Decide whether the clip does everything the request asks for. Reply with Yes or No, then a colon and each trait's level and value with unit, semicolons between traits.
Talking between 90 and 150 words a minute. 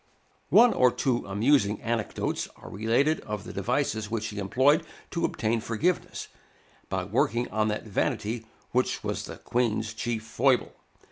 Yes: average, 145 wpm